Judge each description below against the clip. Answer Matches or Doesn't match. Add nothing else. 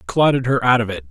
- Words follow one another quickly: Matches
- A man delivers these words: Matches